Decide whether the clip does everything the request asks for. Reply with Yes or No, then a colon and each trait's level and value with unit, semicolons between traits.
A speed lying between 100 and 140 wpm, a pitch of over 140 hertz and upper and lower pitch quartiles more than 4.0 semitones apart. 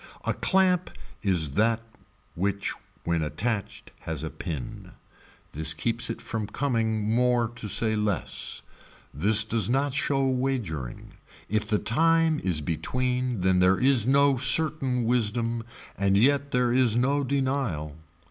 No: slow, 135 wpm; low, 115 Hz; average, 5.1 semitones